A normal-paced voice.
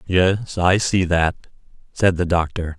Yes: average, 150 wpm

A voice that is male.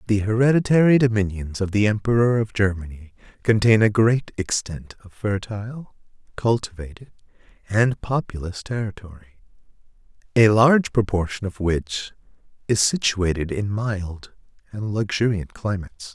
Yes: male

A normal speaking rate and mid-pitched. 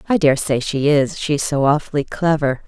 Yes: average, 180 wpm; medium, 150 Hz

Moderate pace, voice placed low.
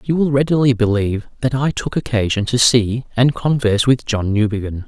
Yes: average, 185 wpm; low, 120 Hz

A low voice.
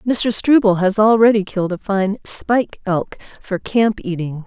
No: high, 205 Hz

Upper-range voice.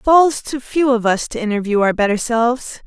Yes: high, 240 Hz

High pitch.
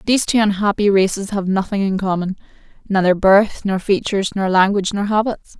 Yes: high, 200 Hz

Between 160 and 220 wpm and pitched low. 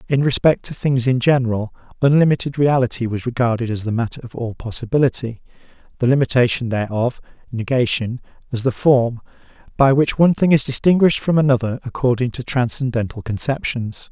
No: average, 150 wpm; low, 125 Hz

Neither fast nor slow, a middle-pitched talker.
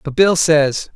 Yes: average, 190 wpm; medium, 155 Hz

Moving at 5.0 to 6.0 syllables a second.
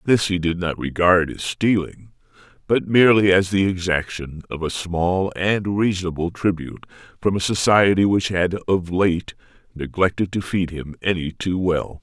No: 4.7 syllables/s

